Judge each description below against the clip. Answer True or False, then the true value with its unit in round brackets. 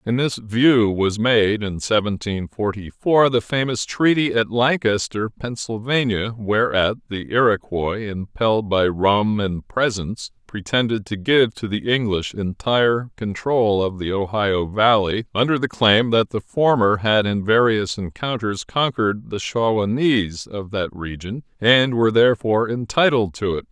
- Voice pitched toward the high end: False (110 Hz)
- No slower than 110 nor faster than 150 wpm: True (145 wpm)